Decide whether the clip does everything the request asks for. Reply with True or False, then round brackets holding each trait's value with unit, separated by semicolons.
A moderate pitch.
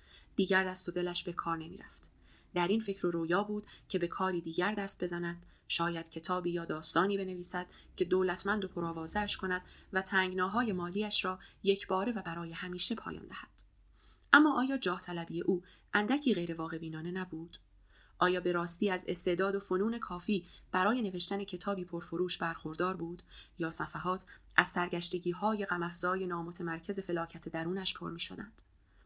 True (180 Hz)